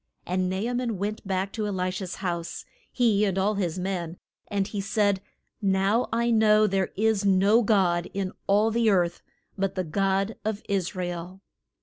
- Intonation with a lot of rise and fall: No, narrow, 2.4 semitones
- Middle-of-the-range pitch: No, high, 195 Hz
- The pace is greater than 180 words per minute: Yes, average, 190 wpm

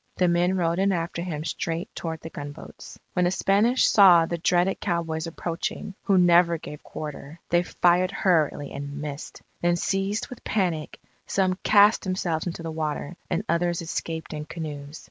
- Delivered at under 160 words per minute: No, average, 165 wpm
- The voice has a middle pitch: Yes, medium, 170 Hz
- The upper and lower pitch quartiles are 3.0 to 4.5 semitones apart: No, narrow, 2.5 semitones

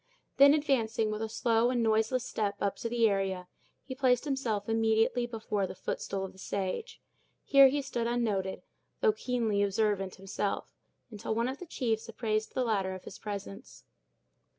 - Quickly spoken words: No, average, 165 wpm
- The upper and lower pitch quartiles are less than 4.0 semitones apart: Yes, average, 3.6 semitones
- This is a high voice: Yes, high, 225 Hz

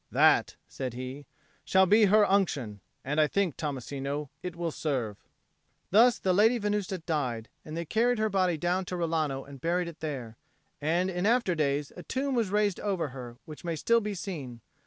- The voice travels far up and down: Yes, wide, 5.9 semitones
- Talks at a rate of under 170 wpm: No, average, 185 wpm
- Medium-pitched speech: Yes, medium, 170 Hz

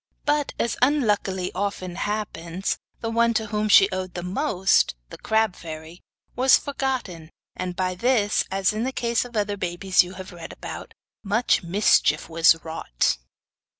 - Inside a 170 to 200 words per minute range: No, average, 155 wpm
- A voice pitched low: No, high, 195 Hz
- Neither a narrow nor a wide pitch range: Yes, average, 4.2 semitones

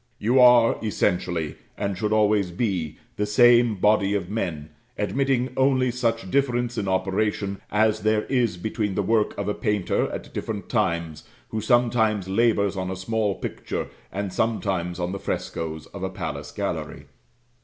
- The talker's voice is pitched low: Yes, low, 105 Hz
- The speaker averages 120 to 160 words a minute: Yes, average, 155 wpm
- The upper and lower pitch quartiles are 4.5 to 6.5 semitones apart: No, average, 3.5 semitones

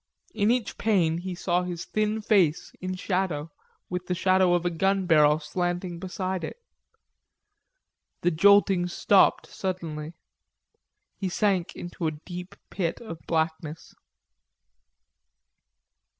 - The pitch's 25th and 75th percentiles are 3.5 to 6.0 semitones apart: No, narrow, 2.5 semitones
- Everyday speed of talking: No, slow, 120 wpm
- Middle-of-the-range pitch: Yes, medium, 180 Hz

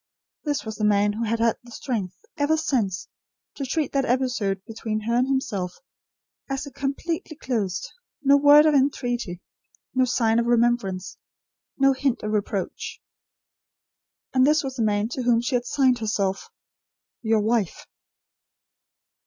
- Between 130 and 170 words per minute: Yes, average, 145 wpm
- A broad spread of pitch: No, average, 4.2 semitones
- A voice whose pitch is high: Yes, high, 240 Hz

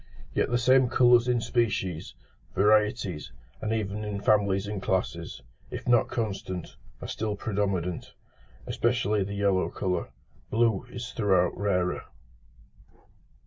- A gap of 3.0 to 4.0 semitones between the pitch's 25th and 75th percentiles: Yes, average, 3.5 semitones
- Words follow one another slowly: Yes, slow, 120 wpm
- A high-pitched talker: No, low, 105 Hz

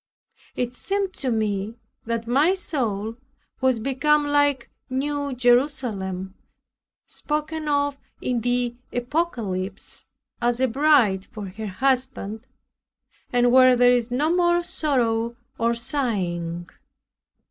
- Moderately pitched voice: No, high, 245 Hz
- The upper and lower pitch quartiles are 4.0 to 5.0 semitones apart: Yes, average, 4.3 semitones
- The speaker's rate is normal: No, slow, 115 wpm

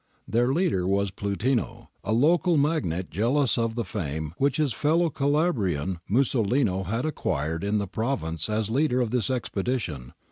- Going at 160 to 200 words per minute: No, average, 150 wpm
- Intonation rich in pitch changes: Yes, wide, 6.3 semitones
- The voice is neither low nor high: No, low, 115 Hz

